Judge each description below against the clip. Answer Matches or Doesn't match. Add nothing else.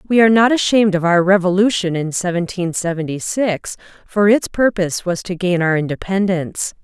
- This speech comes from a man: Doesn't match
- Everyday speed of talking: Matches